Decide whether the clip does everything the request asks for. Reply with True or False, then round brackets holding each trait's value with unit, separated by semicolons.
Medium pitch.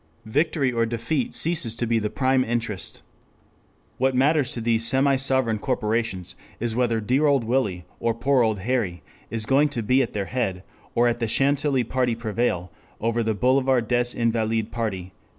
False (120 Hz)